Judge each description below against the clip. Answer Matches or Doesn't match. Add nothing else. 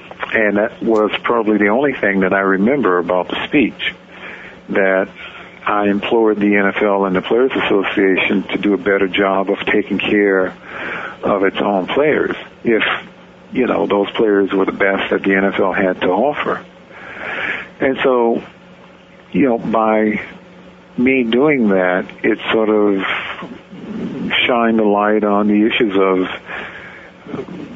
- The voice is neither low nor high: Doesn't match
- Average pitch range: Doesn't match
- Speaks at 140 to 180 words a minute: Matches